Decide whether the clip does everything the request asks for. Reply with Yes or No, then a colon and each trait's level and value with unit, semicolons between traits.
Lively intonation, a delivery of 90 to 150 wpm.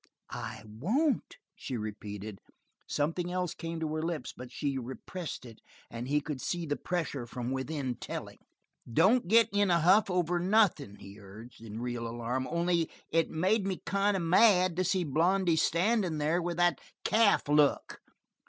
No: wide, 6.2 semitones; average, 165 wpm